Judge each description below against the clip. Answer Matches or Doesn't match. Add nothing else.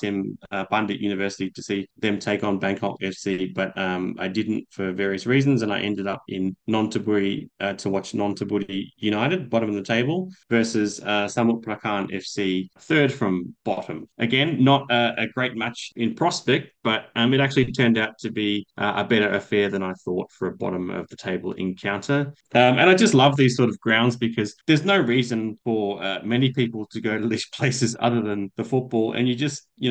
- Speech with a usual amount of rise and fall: Matches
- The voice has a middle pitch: Doesn't match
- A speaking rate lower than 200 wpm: Doesn't match